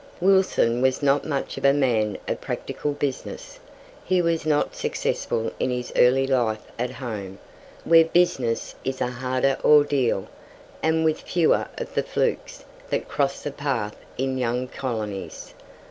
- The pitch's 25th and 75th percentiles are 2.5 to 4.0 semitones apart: Yes, average, 3.3 semitones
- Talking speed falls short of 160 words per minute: Yes, average, 145 wpm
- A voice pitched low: Yes, low, 130 Hz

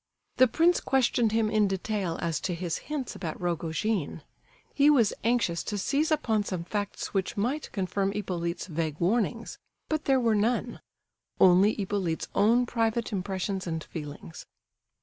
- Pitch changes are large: No, average, 4.9 semitones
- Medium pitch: No, high, 205 Hz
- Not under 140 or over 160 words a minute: Yes, average, 150 wpm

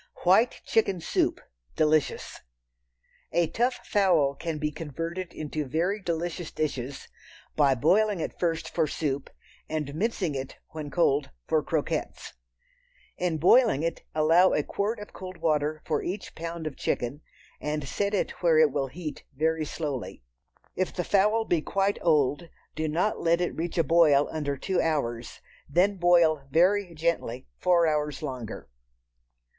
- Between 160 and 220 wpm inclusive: No, average, 150 wpm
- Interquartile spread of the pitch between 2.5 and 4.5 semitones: Yes, average, 3.2 semitones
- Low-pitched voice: No, medium, 160 Hz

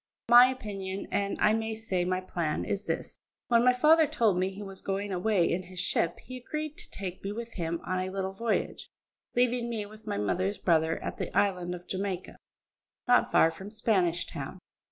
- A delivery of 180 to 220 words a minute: Yes, average, 195 wpm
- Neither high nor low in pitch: No, high, 195 Hz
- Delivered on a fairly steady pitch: No, average, 3.9 semitones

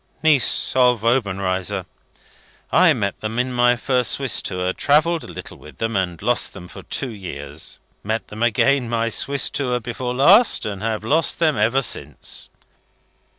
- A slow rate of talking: No, average, 160 wpm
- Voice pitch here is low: Yes, low, 120 Hz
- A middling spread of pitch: Yes, average, 4.8 semitones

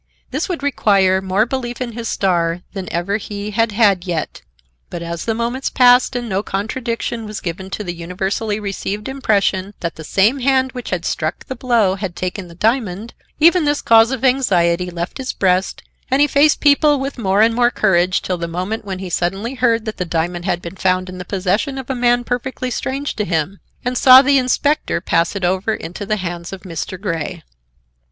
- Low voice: No, high, 205 Hz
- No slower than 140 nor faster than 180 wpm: No, fast, 205 wpm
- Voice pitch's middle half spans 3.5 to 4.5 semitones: No, average, 5.2 semitones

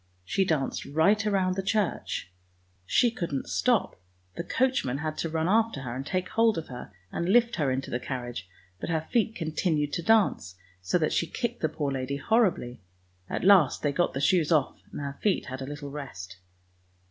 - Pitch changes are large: Yes, wide, 6.3 semitones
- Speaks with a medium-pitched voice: Yes, medium, 160 Hz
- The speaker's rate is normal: Yes, average, 195 wpm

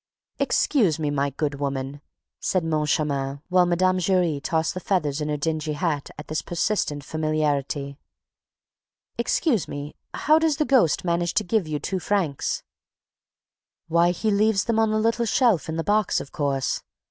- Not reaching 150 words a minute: No, average, 165 wpm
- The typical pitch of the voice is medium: Yes, medium, 165 Hz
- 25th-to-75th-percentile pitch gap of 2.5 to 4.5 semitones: No, wide, 5.4 semitones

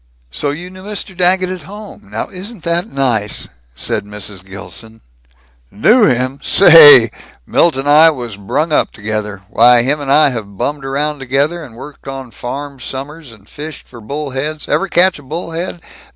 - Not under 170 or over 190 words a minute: Yes, average, 175 wpm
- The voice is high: No, medium, 140 Hz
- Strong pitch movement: Yes, wide, 6.0 semitones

